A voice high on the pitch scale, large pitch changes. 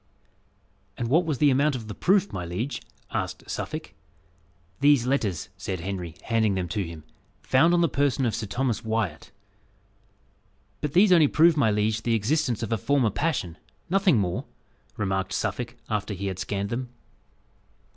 No: low, 115 Hz; wide, 6.3 semitones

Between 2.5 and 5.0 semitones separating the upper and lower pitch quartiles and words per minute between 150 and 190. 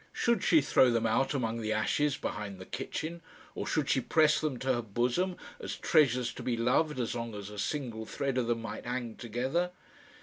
No: average, 4.5 semitones; fast, 205 wpm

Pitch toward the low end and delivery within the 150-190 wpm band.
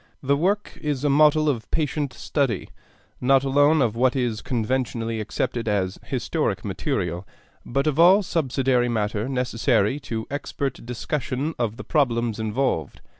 No: low, 130 Hz; average, 140 wpm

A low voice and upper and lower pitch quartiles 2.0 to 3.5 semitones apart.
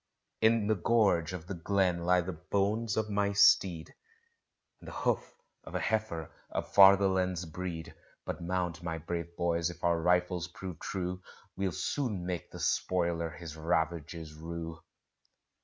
Yes: very low, 90 Hz; narrow, 2.6 semitones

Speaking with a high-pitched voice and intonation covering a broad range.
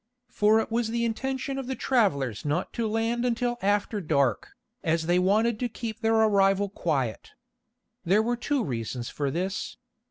Yes: high, 215 Hz; wide, 5.7 semitones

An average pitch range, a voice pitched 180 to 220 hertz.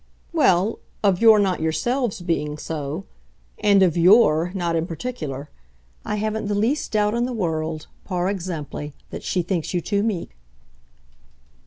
Yes: average, 4.6 semitones; medium, 185 Hz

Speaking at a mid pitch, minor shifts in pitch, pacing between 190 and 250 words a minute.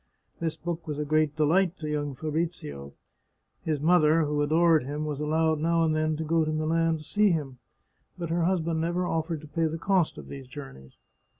Yes: medium, 155 Hz; narrow, 1.7 semitones; average, 200 wpm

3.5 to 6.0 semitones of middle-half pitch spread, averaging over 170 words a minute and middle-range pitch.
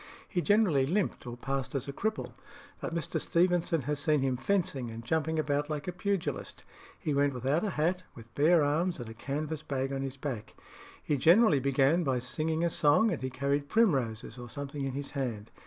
Yes: average, 3.8 semitones; average, 200 wpm; medium, 145 Hz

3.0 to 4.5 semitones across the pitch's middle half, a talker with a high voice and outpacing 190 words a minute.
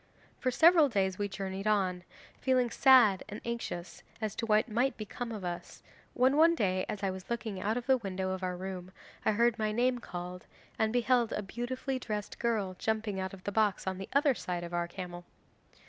Yes: average, 4.2 semitones; high, 210 Hz; fast, 205 wpm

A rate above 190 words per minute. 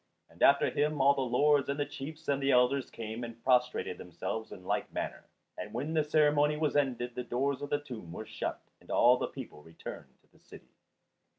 Yes: fast, 205 wpm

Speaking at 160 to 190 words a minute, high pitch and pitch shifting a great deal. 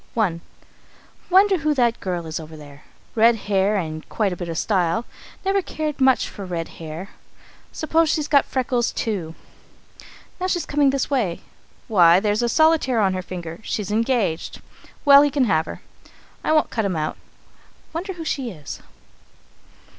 Yes: average, 165 wpm; high, 220 Hz; wide, 8.5 semitones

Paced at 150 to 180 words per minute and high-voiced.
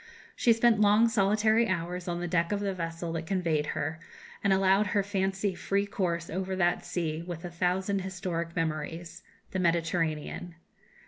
No: average, 165 wpm; medium, 180 Hz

